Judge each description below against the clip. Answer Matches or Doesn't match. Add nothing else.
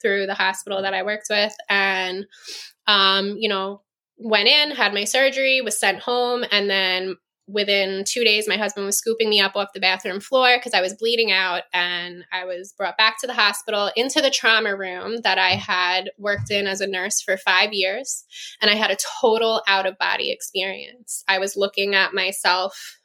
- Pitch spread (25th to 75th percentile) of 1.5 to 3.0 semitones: Matches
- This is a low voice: Doesn't match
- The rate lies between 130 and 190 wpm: Doesn't match